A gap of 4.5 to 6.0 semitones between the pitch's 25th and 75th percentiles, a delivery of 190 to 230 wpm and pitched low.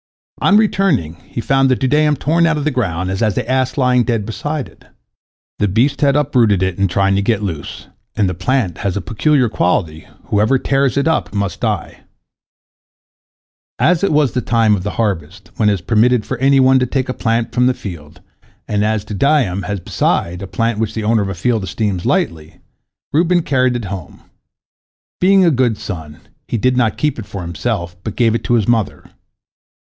Yes: average, 5.3 semitones; average, 200 wpm; low, 115 Hz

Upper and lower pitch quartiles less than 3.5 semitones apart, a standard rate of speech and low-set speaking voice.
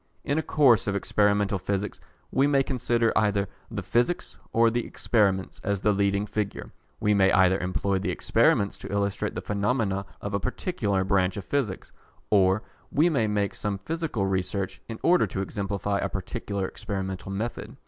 Yes: average, 2.8 semitones; average, 170 wpm; low, 100 Hz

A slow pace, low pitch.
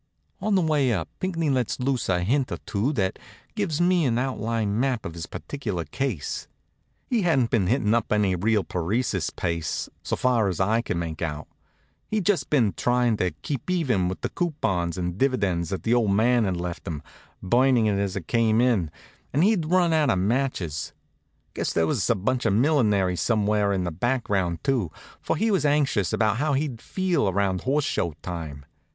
No: average, 190 wpm; low, 110 Hz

